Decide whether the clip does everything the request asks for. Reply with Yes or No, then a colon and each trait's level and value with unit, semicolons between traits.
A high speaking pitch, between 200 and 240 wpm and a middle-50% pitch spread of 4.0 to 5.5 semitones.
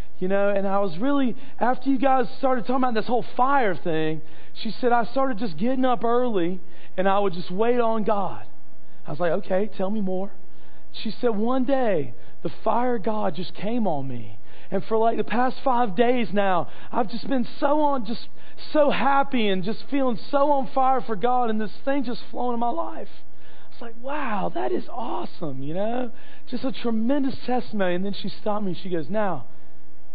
Yes: high, 225 Hz; fast, 205 wpm; average, 4.9 semitones